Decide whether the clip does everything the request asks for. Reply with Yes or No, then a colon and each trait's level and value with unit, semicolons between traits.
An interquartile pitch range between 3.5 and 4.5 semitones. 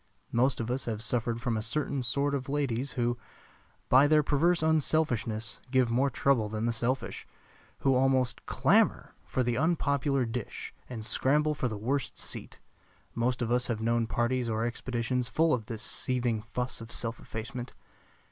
No: average, 2.9 semitones